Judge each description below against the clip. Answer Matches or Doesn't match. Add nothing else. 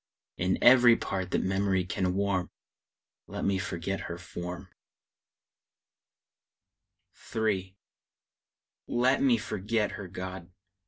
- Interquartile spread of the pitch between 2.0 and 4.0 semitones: Matches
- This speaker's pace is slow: Matches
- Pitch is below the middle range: Matches